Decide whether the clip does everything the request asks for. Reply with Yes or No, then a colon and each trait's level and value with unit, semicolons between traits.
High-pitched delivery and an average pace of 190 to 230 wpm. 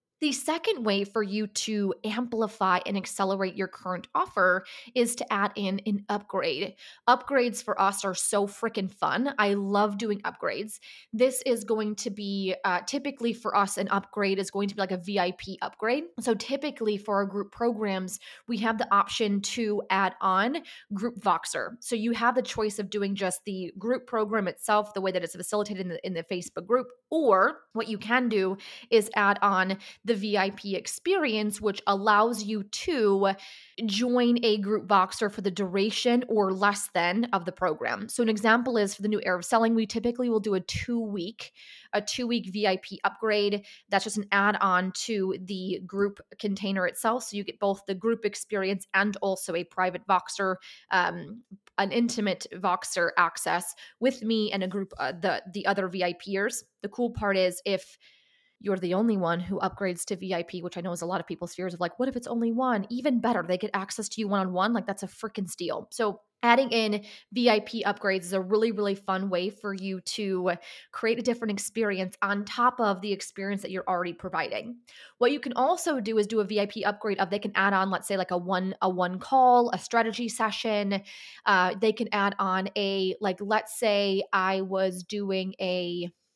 Yes: high, 205 Hz; average, 195 wpm